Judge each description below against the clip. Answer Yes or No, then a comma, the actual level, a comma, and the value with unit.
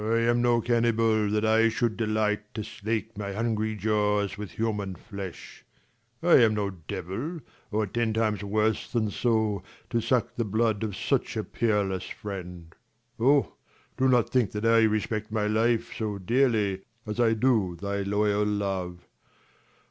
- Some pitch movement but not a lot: No, narrow, 2.0 semitones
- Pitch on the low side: Yes, low, 110 Hz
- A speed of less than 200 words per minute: Yes, average, 165 wpm